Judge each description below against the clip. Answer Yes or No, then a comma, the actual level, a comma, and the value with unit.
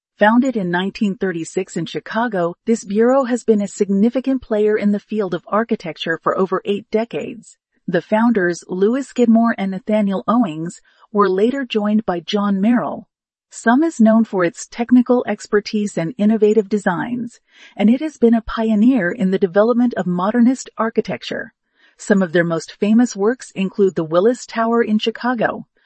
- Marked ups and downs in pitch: No, average, 3.5 semitones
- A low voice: No, high, 215 Hz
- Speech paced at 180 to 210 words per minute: No, average, 160 wpm